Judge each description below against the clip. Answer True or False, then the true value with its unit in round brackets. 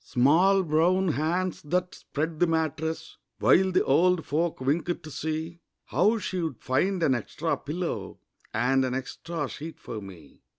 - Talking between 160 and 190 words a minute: False (145 wpm)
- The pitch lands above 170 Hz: False (160 Hz)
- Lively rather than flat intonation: False (4.1 semitones)